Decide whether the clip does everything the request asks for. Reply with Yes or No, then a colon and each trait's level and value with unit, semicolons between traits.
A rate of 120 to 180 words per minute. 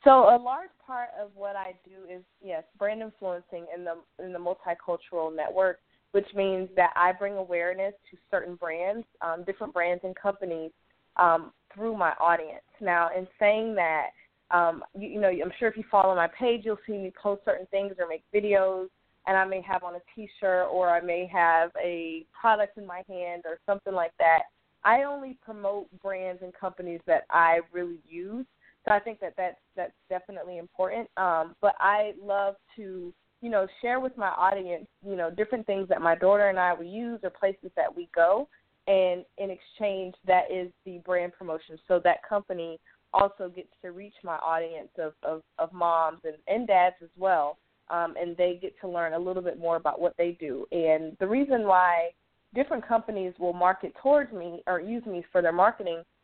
No: average, 195 wpm